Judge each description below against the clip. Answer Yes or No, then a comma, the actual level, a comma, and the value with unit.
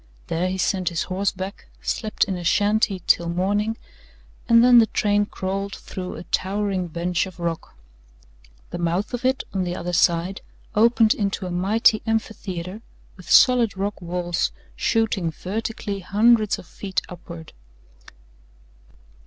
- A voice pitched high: Yes, high, 195 Hz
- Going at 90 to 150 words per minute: Yes, average, 145 wpm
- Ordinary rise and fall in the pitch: Yes, average, 3.3 semitones